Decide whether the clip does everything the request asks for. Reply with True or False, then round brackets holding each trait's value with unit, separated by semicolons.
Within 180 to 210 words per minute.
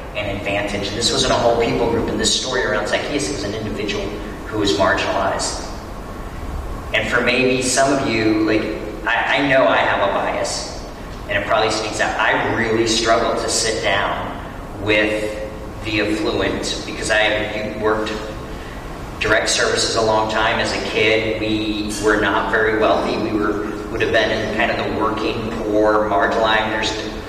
False (170 wpm)